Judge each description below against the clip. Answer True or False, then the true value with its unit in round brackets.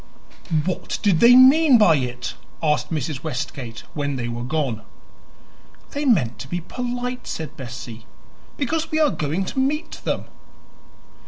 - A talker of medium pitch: True (160 Hz)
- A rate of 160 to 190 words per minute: False (145 wpm)